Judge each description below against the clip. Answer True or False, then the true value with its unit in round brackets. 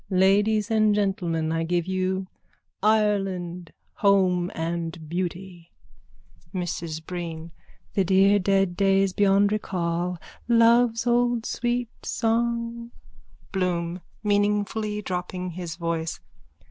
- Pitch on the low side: False (190 Hz)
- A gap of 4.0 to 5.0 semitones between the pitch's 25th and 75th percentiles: False (3.2 semitones)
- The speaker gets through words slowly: True (100 wpm)